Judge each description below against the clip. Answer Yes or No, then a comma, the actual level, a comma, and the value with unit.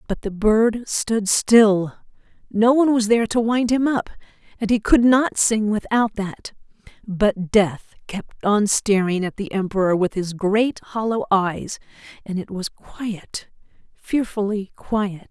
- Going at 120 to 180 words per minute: Yes, average, 150 wpm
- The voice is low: No, high, 210 Hz